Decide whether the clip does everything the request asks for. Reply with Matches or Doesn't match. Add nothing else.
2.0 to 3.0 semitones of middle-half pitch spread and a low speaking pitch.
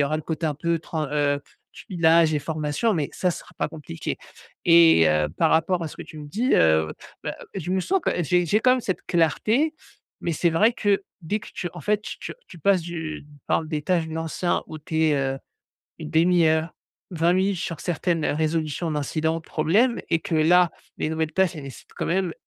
Doesn't match